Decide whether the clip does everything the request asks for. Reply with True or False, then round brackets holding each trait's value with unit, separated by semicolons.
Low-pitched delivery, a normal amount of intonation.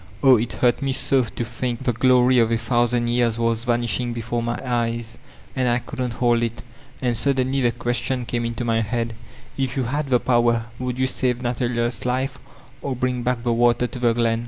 False (120 Hz; 1.4 semitones)